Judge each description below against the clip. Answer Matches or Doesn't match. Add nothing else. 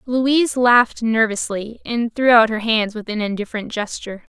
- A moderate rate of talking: Matches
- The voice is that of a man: Doesn't match